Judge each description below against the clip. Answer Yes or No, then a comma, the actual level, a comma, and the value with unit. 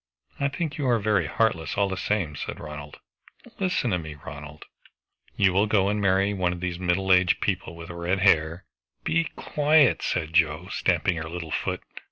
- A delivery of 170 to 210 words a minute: Yes, average, 185 wpm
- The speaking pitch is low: Yes, very low, 90 Hz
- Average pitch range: Yes, average, 3.9 semitones